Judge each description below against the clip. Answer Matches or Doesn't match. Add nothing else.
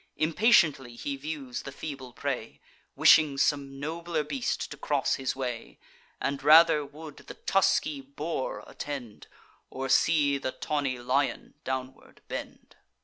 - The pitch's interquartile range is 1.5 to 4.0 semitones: Matches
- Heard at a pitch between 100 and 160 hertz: Matches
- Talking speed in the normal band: Doesn't match